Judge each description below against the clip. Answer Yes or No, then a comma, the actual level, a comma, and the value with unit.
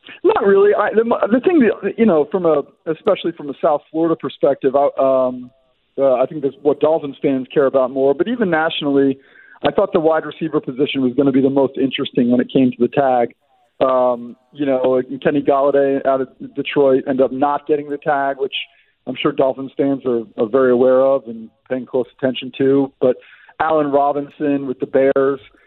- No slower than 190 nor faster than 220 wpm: Yes, average, 200 wpm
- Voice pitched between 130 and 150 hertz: Yes, medium, 140 Hz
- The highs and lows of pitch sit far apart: No, average, 2.8 semitones